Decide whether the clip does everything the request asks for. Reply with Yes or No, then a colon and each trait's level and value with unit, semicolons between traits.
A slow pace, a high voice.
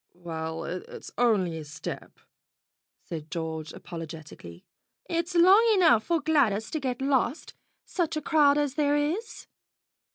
Yes: slow, 130 wpm; high, 245 Hz